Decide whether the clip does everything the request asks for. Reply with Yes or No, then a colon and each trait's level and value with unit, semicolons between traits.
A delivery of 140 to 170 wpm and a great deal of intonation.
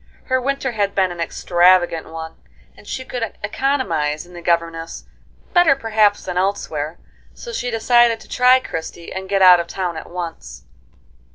Yes: average, 165 wpm; wide, 6.1 semitones